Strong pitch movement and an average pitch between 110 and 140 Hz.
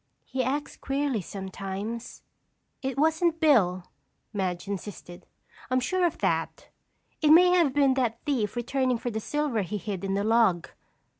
No: wide, 6.3 semitones; high, 240 Hz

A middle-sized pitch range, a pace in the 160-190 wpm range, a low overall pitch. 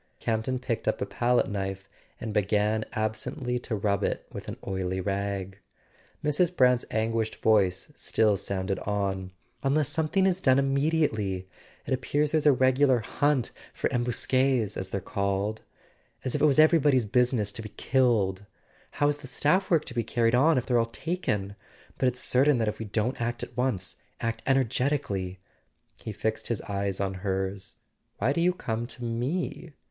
Yes: average, 5.0 semitones; average, 175 wpm; low, 115 Hz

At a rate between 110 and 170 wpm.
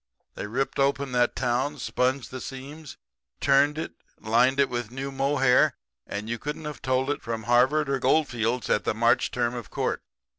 No: average, 180 wpm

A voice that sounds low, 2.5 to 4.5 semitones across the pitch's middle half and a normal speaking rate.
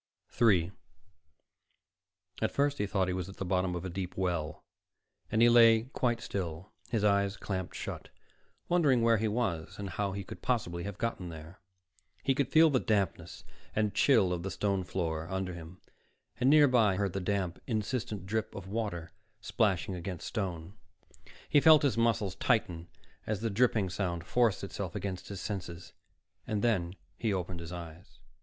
Yes: low, 100 Hz; average, 4.2 semitones; average, 170 wpm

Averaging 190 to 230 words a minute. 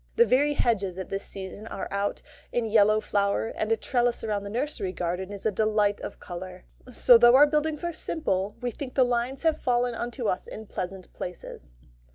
Yes: average, 200 wpm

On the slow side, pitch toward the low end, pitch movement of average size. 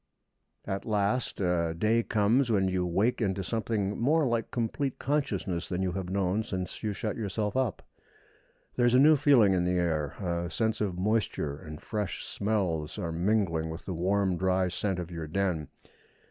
No: average, 175 wpm; very low, 95 Hz; average, 4.0 semitones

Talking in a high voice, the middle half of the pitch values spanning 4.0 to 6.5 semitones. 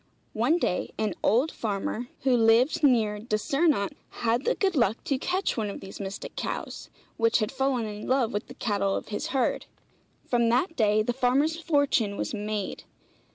Yes: high, 235 Hz; average, 4.3 semitones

